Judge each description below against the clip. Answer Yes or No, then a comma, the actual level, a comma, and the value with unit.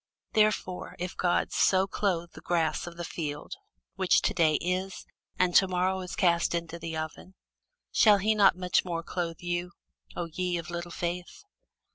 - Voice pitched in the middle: Yes, medium, 175 Hz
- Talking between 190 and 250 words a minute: No, average, 170 wpm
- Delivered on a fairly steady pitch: Yes, narrow, 1.6 semitones